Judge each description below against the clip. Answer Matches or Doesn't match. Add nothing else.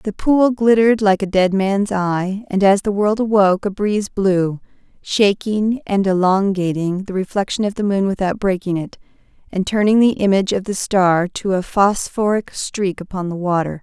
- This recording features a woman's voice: Matches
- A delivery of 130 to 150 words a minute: Doesn't match